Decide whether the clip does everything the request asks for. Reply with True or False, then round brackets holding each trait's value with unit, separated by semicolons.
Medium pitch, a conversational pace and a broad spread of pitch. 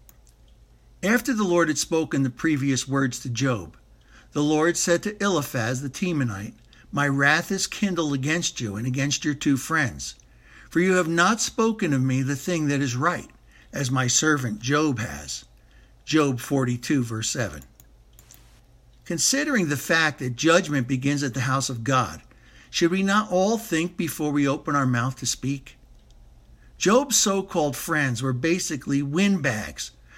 False (145 Hz; 155 wpm; 4.7 semitones)